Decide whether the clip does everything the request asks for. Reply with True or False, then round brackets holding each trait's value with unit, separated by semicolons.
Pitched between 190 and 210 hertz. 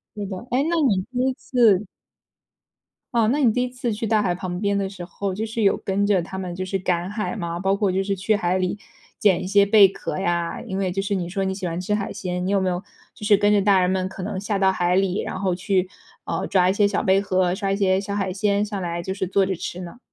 True (195 Hz)